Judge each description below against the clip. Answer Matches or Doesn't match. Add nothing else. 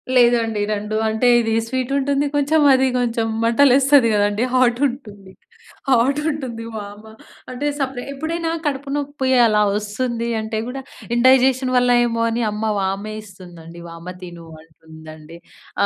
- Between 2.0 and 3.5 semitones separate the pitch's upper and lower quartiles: Doesn't match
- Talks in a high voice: Matches